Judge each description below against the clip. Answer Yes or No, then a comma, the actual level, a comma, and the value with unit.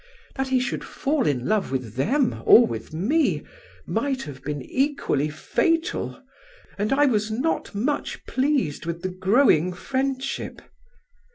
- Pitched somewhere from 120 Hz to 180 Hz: No, high, 230 Hz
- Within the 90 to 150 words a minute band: Yes, average, 140 wpm